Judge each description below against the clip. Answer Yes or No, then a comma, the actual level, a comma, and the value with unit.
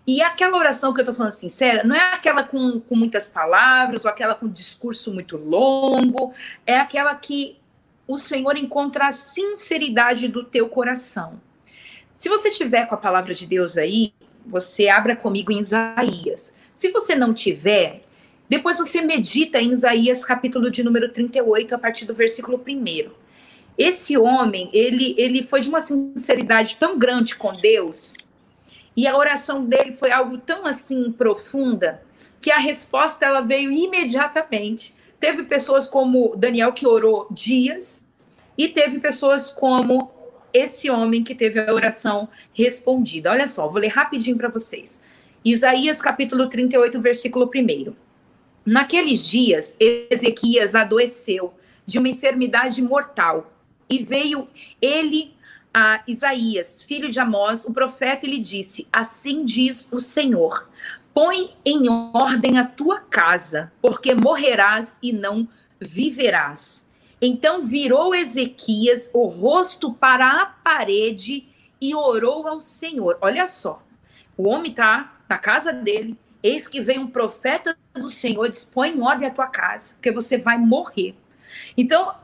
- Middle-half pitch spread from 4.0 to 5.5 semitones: No, average, 3.6 semitones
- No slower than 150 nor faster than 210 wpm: No, average, 140 wpm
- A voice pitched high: Yes, very high, 255 Hz